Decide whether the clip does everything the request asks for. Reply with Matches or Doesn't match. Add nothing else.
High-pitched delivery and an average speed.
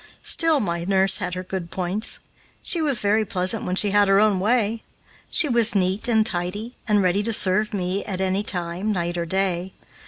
Matches